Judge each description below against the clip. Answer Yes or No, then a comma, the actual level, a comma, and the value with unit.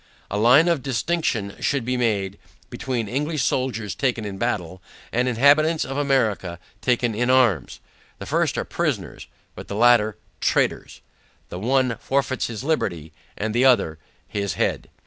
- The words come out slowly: No, average, 145 wpm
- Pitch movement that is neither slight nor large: Yes, average, 4.3 semitones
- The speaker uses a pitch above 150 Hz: No, low, 120 Hz